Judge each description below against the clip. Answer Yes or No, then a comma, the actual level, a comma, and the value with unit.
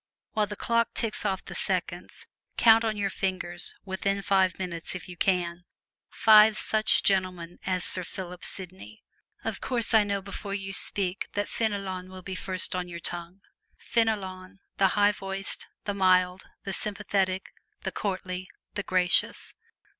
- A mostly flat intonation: Yes, narrow, 1.9 semitones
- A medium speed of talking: Yes, average, 155 wpm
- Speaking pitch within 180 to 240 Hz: Yes, high, 190 Hz